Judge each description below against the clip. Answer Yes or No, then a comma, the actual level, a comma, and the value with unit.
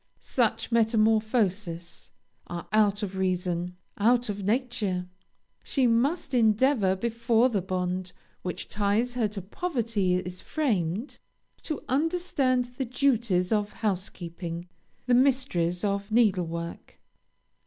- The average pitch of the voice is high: Yes, high, 210 Hz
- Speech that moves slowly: Yes, slow, 110 wpm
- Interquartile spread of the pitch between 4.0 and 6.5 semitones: Yes, average, 5.0 semitones